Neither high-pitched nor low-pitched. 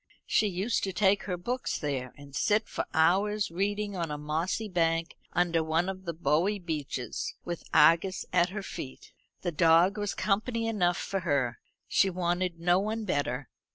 Yes: medium, 175 Hz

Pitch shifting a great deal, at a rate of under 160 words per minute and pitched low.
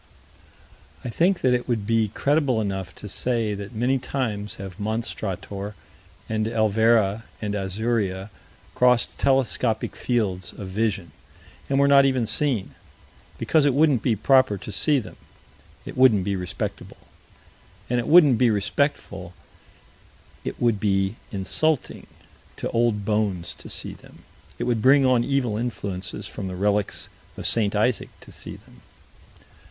No: average, 3.9 semitones; average, 145 wpm; low, 110 Hz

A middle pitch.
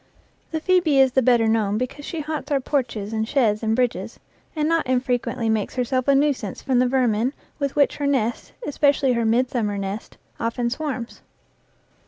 No: very high, 255 Hz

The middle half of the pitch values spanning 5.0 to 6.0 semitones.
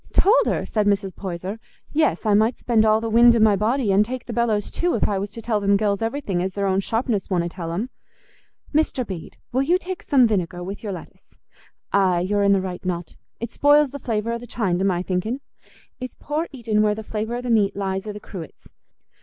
No: average, 3.7 semitones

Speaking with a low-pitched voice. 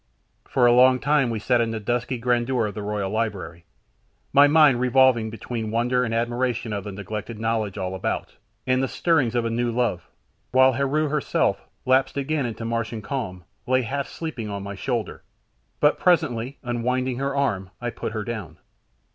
Yes: low, 120 Hz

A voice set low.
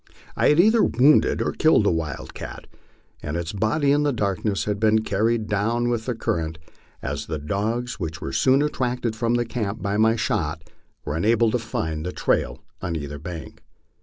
Yes: low, 110 Hz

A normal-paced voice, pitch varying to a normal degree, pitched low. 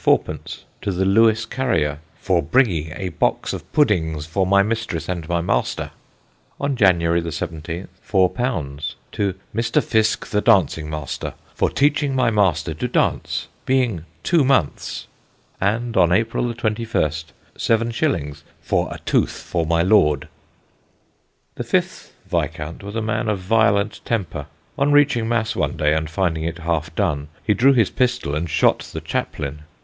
No: average, 150 wpm; wide, 6.1 semitones; very low, 95 Hz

